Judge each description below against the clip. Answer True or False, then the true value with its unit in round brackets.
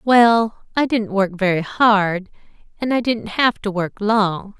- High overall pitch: True (210 Hz)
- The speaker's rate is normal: True (170 wpm)